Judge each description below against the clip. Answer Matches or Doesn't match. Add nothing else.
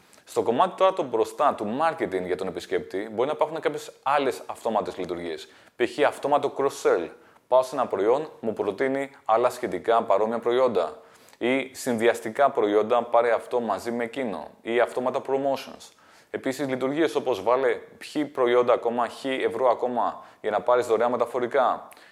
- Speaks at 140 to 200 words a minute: Matches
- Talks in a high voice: Doesn't match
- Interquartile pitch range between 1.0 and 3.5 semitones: Matches